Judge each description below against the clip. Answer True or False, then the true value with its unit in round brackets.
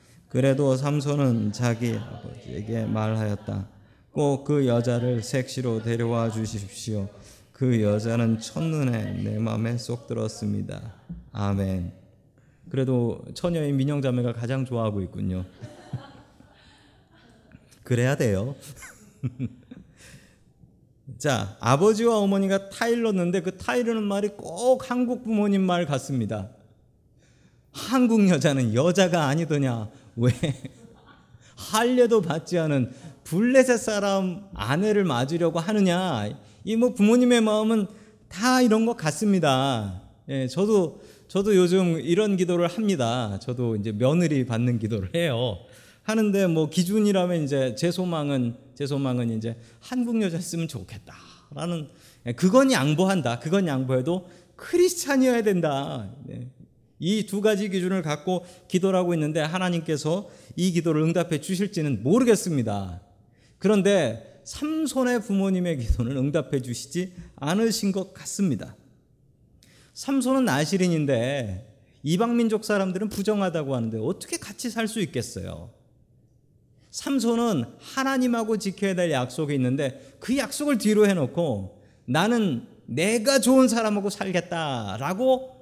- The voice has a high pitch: False (155 Hz)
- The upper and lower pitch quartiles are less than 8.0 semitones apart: False (8.6 semitones)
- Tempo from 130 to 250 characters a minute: False (270 characters per minute)